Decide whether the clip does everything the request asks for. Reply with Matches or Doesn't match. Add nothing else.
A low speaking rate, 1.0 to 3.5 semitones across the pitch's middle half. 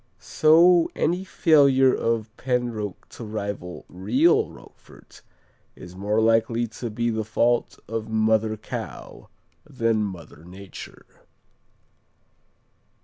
Matches